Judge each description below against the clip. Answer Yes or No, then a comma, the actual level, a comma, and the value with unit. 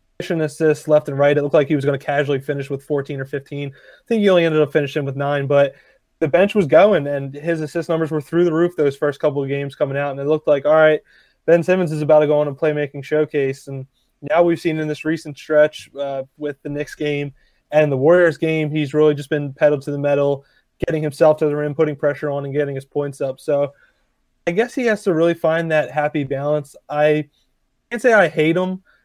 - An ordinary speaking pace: No, fast, 240 wpm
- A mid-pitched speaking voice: Yes, medium, 150 Hz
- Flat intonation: Yes, narrow, 2.0 semitones